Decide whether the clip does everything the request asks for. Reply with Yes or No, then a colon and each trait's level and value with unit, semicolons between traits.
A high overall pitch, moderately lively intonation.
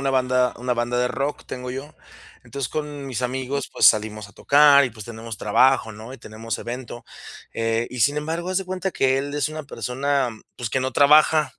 No: low, 130 Hz; average, 3.3 semitones